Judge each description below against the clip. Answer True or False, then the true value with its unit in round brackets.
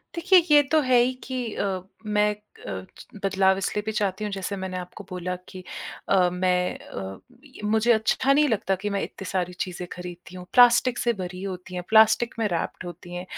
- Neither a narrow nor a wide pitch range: True (3.4 semitones)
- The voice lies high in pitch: True (195 Hz)